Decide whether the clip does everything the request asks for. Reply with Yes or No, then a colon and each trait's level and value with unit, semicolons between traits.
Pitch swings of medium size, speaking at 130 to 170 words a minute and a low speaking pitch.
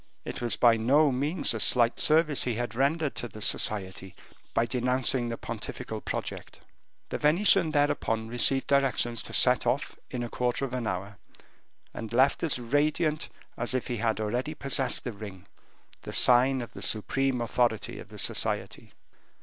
Yes: average, 3.3 semitones; average, 160 wpm; low, 125 Hz